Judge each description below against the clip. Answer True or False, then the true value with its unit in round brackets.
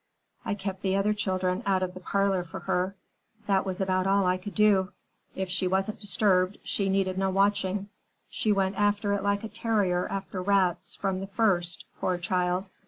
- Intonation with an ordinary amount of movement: False (1.6 semitones)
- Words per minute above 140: True (185 wpm)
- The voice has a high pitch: True (195 Hz)